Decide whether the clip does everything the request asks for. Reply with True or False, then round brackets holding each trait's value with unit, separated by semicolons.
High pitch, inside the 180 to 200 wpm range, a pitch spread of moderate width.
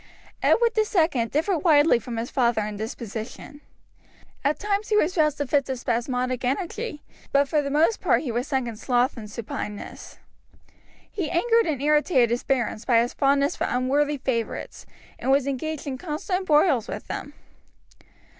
False (275 Hz; 165 wpm; 4.4 semitones)